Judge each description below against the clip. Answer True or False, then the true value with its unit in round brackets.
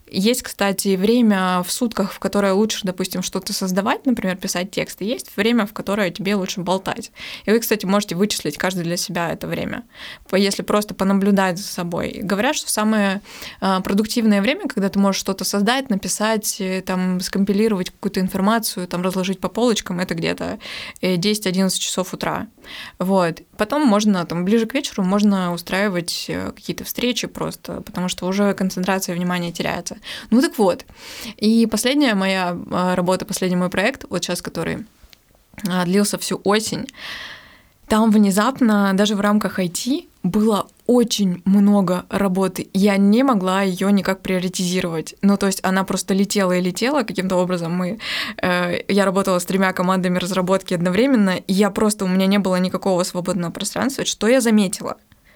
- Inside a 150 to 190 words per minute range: True (155 wpm)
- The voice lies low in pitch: False (195 Hz)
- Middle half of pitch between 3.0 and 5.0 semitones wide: False (2.6 semitones)